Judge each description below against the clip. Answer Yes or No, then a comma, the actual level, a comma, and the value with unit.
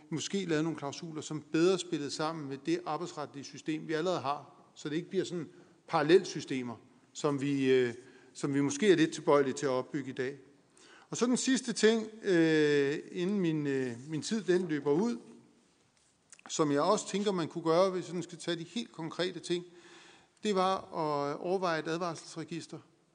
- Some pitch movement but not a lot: Yes, average, 3.6 semitones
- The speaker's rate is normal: Yes, average, 175 wpm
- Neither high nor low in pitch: Yes, medium, 160 Hz